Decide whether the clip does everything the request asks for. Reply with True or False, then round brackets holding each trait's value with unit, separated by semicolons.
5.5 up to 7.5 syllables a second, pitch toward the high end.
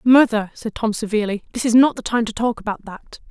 True (6.0 syllables/s; 225 Hz)